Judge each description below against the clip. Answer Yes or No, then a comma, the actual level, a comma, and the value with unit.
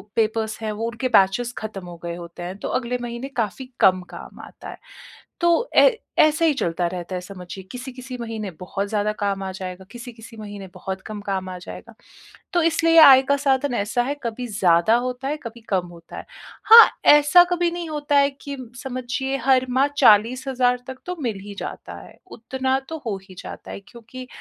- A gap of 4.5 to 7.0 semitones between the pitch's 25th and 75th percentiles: Yes, average, 5.2 semitones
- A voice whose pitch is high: Yes, high, 235 Hz